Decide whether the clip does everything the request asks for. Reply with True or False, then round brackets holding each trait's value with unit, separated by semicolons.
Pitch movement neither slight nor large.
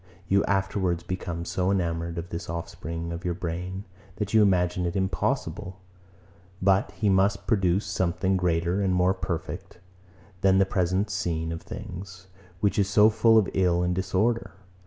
False (2.1 semitones)